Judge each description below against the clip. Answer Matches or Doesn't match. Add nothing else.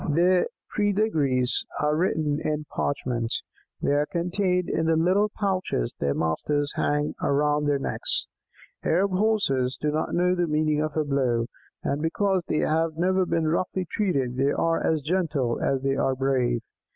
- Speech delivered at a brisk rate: Doesn't match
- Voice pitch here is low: Doesn't match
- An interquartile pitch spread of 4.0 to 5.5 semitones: Matches